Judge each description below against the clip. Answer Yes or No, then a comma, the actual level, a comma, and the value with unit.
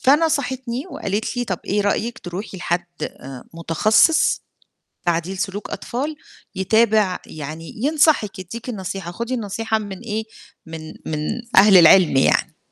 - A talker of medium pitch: No, high, 205 Hz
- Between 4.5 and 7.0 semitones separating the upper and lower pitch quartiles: Yes, average, 5.0 semitones